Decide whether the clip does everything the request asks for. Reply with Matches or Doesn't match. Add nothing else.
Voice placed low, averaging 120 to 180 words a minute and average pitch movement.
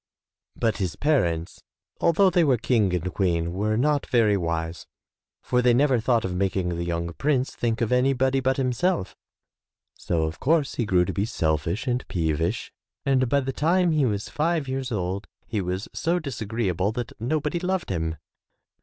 Doesn't match